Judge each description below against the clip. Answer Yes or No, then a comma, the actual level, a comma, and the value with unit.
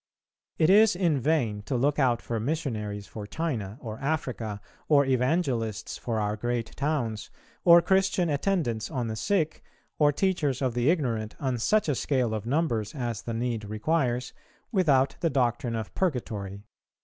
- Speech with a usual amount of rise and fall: No, wide, 5.7 semitones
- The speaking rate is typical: Yes, average, 160 wpm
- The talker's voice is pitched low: Yes, low, 125 Hz